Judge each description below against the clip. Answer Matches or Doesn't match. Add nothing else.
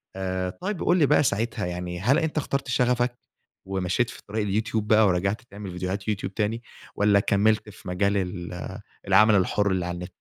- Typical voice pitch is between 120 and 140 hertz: Doesn't match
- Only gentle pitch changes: Doesn't match